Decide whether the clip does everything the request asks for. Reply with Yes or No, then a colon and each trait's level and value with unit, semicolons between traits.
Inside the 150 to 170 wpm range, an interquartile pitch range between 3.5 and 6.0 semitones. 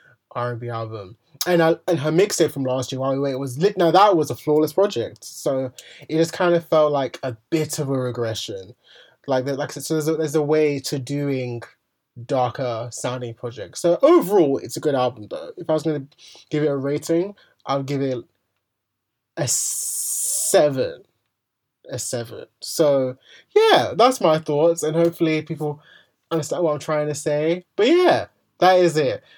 No: average, 185 wpm; average, 4.1 semitones